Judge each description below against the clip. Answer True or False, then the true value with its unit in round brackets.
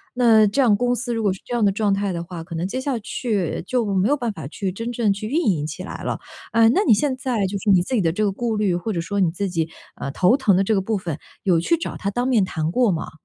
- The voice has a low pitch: False (205 Hz)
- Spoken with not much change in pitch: False (4.5 semitones)